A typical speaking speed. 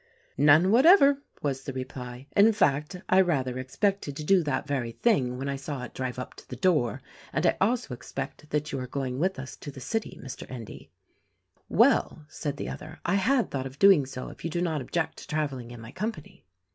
No: fast, 210 wpm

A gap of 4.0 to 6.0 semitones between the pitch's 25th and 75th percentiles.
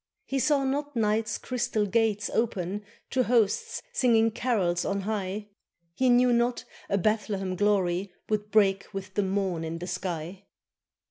No: average, 3.4 semitones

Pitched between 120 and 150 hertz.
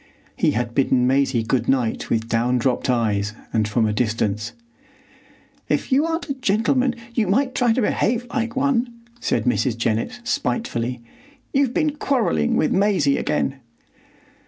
Yes: medium, 140 Hz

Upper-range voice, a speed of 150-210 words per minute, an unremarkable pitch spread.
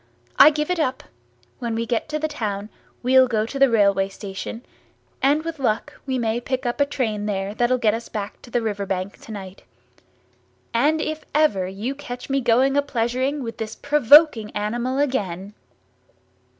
Yes: high, 240 Hz; average, 170 wpm; average, 4.8 semitones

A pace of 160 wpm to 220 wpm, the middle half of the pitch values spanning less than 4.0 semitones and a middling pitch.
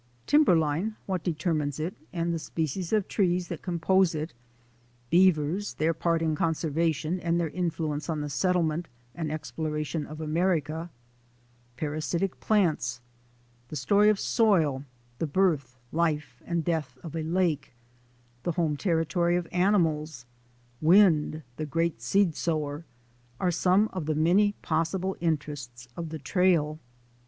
No: average, 140 wpm; average, 2.8 semitones; medium, 165 Hz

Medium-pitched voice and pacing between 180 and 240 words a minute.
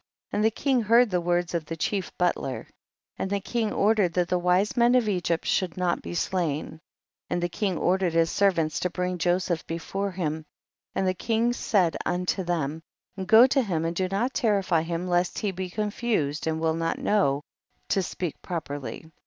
Yes: medium, 180 Hz; fast, 205 wpm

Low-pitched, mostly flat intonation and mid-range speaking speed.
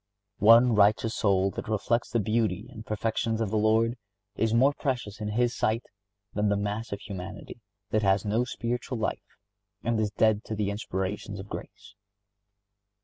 Yes: low, 110 Hz; narrow, 2.1 semitones; average, 165 wpm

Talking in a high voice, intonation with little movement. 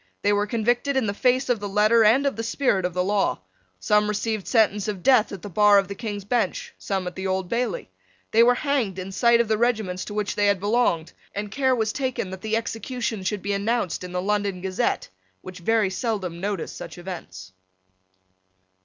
No: high, 210 Hz; average, 3.4 semitones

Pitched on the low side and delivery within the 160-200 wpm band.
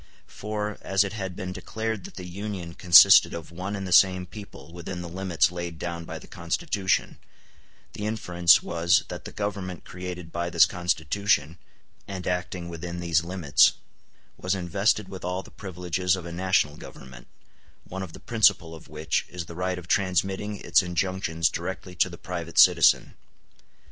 Yes: very low, 90 Hz; average, 170 wpm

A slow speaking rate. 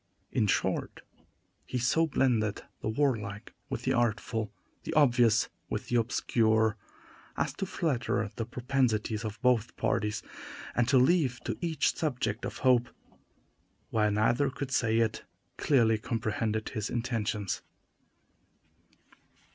Yes: slow, 125 wpm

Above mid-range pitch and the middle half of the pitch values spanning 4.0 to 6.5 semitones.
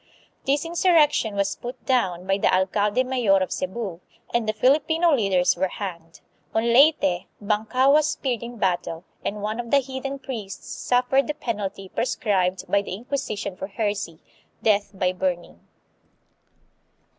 Yes: high, 215 Hz; average, 5.3 semitones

